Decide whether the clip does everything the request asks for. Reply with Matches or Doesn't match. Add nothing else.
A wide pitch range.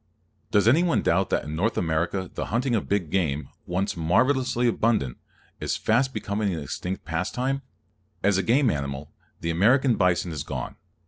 Matches